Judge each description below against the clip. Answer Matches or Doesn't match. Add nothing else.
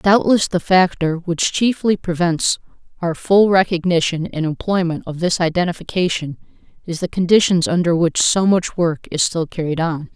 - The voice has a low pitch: Doesn't match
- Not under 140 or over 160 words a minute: Matches